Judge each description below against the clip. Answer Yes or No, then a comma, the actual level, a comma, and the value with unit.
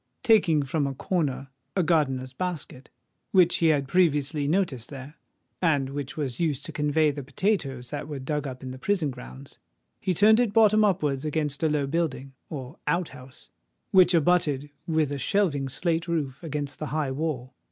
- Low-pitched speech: No, medium, 150 Hz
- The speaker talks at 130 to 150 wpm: No, average, 175 wpm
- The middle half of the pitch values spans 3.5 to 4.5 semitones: Yes, average, 3.8 semitones